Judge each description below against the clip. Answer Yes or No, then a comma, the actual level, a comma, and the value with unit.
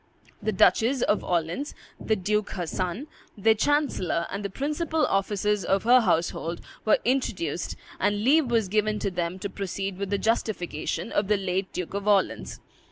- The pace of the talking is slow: No, average, 165 wpm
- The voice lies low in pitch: No, high, 200 Hz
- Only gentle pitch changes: No, average, 3.4 semitones